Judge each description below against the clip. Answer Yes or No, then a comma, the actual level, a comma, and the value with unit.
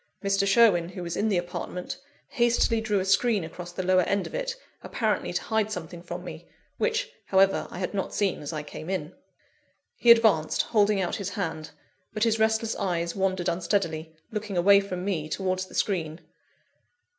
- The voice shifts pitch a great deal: No, average, 3.5 semitones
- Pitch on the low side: No, high, 190 Hz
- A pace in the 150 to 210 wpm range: Yes, average, 180 wpm